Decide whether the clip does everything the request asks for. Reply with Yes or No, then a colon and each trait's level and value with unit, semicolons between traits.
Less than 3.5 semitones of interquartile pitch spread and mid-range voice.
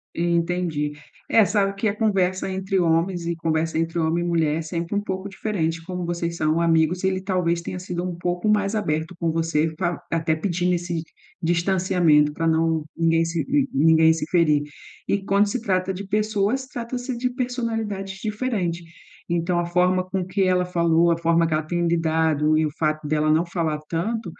Yes: average, 2.9 semitones; medium, 175 Hz